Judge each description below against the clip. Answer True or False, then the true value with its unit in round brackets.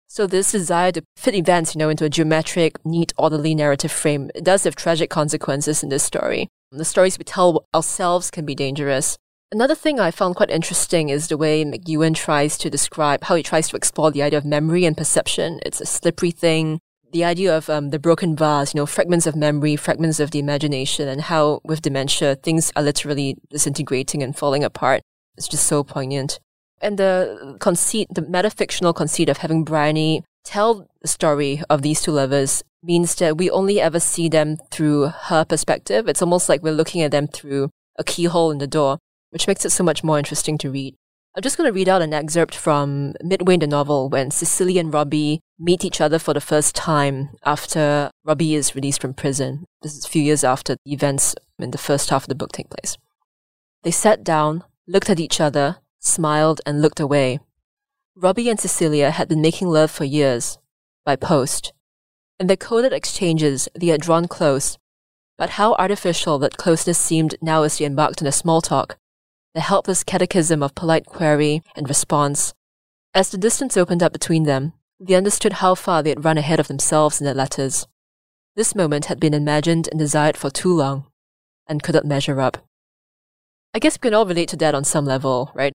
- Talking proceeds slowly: False (200 wpm)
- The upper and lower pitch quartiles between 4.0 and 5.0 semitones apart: False (3.0 semitones)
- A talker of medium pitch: True (155 Hz)